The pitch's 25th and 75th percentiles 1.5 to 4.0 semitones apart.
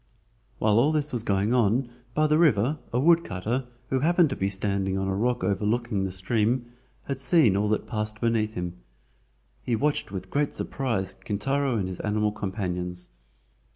No: average, 5.2 semitones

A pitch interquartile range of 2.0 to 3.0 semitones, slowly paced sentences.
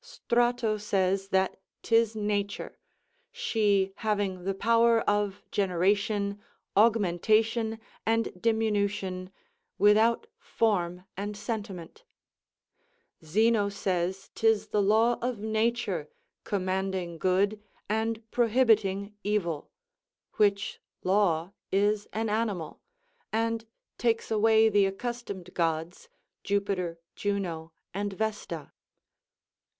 Yes: average, 2.7 semitones; slow, 90 wpm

